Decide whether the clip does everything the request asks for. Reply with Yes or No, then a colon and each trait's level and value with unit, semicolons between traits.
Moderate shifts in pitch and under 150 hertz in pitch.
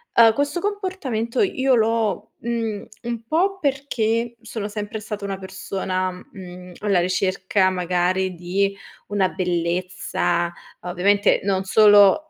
No: average, 3.7 semitones; high, 205 Hz